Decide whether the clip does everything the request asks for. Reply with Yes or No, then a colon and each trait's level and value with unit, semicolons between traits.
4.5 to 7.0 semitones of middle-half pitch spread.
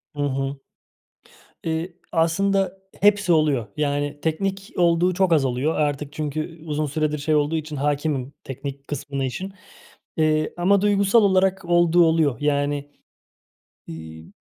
No: average, 3.5 semitones